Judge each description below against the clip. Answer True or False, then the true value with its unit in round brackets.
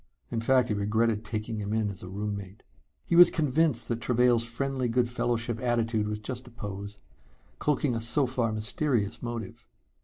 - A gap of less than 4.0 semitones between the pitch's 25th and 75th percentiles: True (2.7 semitones)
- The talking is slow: False (175 wpm)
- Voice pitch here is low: True (115 Hz)